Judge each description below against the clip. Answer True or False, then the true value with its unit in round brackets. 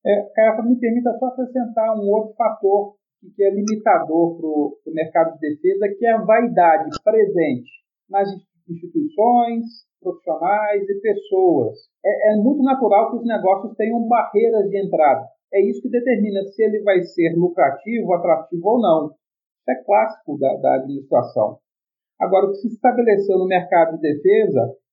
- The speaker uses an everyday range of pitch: True (4.6 semitones)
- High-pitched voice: True (210 Hz)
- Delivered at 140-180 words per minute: True (155 wpm)